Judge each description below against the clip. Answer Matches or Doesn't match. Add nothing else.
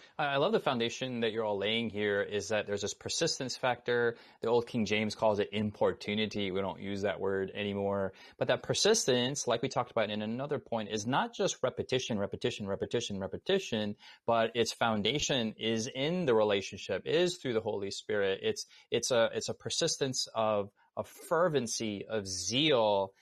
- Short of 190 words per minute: Matches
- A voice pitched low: Matches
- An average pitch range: Matches